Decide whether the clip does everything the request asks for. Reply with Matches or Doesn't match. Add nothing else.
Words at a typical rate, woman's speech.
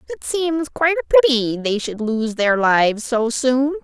Matches